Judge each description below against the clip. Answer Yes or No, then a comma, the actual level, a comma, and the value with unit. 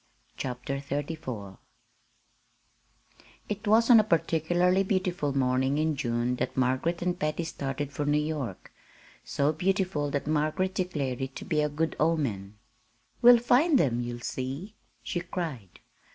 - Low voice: No, medium, 150 Hz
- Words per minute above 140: No, slow, 135 wpm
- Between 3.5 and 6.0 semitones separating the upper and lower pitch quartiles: Yes, average, 5.3 semitones